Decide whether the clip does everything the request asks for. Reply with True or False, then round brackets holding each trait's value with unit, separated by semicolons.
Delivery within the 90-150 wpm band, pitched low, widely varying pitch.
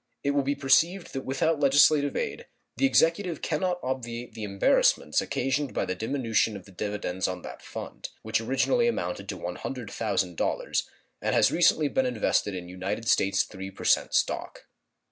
False (160 wpm; 130 Hz; 6.6 semitones)